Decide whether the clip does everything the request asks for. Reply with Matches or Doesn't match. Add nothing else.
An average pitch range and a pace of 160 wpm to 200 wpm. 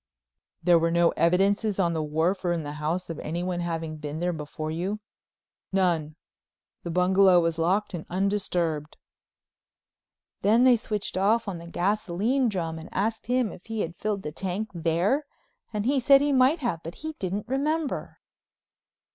Matches